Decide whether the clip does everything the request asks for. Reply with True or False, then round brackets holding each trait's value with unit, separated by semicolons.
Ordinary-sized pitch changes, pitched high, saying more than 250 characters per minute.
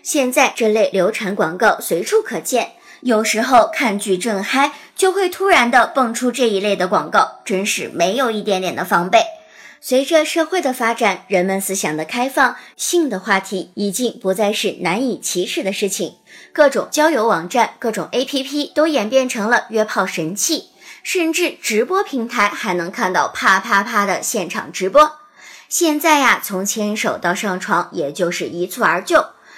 False (6.9 semitones; 225 Hz; 260 characters per minute)